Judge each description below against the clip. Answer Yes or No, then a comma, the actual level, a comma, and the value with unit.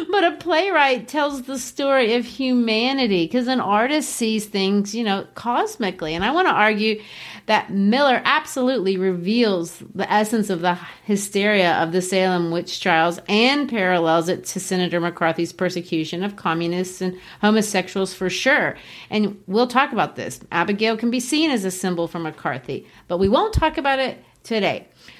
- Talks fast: No, average, 165 wpm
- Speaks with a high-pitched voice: Yes, high, 205 Hz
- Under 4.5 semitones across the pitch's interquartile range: No, average, 5.2 semitones